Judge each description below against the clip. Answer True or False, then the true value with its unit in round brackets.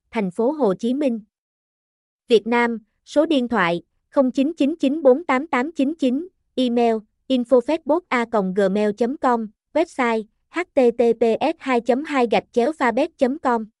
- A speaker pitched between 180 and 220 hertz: False (250 Hz)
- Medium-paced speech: False (65 wpm)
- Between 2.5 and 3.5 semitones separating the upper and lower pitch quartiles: True (3.2 semitones)